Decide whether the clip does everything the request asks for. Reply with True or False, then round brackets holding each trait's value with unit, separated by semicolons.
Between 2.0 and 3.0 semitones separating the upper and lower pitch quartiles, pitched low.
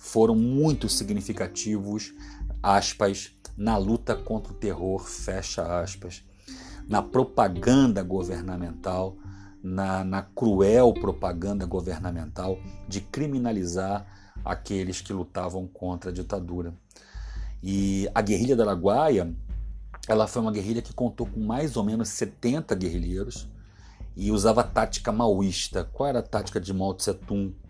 True (2.7 semitones; 100 Hz)